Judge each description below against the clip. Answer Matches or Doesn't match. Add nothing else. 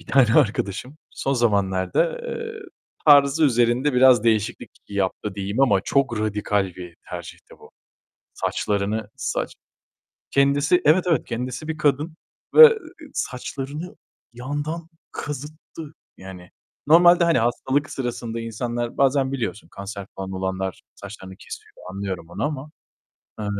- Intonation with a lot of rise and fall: Matches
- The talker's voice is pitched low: Matches